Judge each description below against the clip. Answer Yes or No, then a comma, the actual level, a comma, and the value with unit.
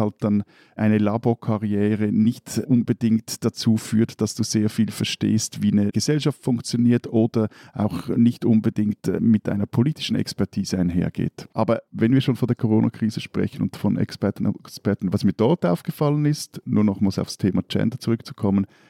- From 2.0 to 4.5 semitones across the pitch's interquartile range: Yes, narrow, 2.4 semitones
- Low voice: Yes, low, 110 Hz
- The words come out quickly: No, average, 160 wpm